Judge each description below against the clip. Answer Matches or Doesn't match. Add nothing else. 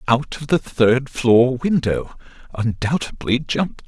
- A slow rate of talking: Matches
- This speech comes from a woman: Doesn't match